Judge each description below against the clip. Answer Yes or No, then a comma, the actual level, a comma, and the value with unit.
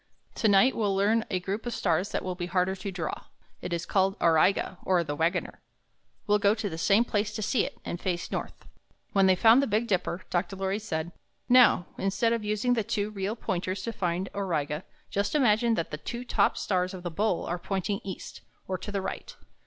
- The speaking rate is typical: No, fast, 220 wpm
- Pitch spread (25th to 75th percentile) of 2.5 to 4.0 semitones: Yes, average, 3.0 semitones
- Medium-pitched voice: No, high, 195 Hz